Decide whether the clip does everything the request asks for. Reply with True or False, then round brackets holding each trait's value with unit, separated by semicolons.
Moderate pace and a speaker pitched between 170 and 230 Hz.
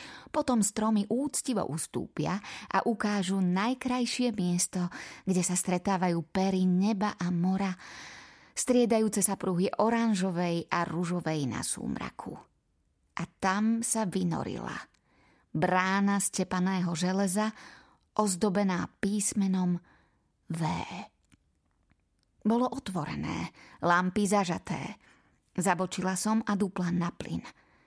False (95 wpm; 190 Hz)